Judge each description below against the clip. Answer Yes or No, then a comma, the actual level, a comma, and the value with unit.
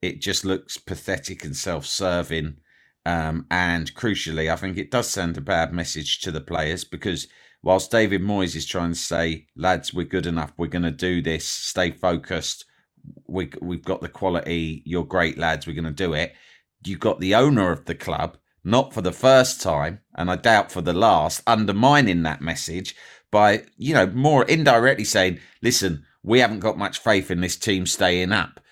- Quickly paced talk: No, average, 190 wpm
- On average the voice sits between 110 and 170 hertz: No, very low, 90 Hz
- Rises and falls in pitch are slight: No, average, 3.6 semitones